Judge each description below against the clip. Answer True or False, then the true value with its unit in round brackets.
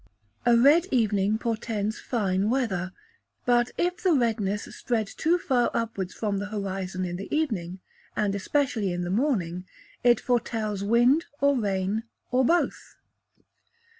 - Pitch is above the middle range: True (220 Hz)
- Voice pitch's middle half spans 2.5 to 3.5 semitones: False (4.3 semitones)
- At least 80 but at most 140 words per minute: True (135 wpm)